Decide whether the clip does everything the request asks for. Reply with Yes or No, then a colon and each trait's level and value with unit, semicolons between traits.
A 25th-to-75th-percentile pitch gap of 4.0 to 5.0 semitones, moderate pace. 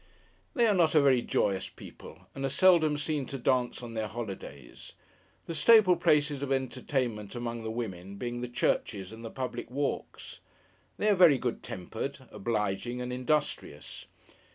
Yes: average, 4.6 semitones; average, 160 wpm